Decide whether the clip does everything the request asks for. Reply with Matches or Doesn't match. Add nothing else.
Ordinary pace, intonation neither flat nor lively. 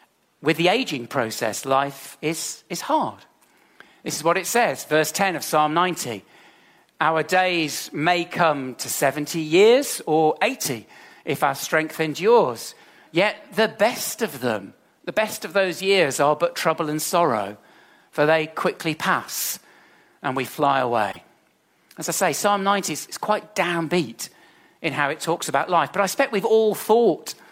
Matches